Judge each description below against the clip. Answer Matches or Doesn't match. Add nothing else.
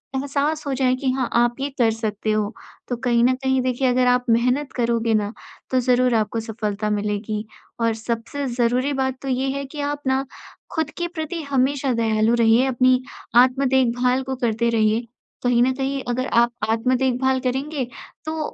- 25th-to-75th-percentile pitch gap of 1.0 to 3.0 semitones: Matches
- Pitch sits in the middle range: Doesn't match